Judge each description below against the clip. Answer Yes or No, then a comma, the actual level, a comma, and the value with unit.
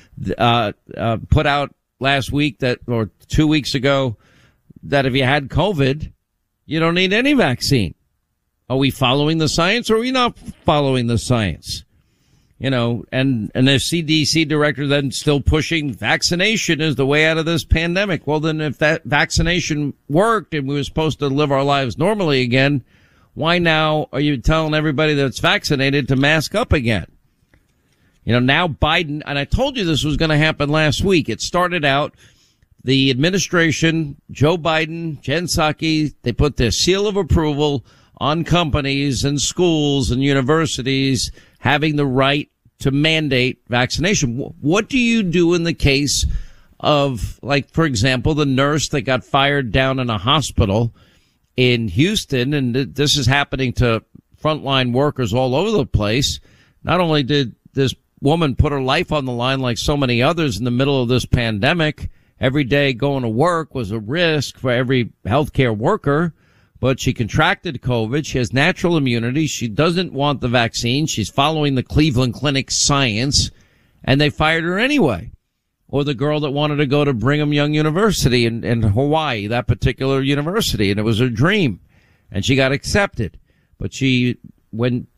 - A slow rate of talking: No, average, 170 wpm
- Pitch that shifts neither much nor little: Yes, average, 3.7 semitones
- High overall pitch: No, medium, 140 Hz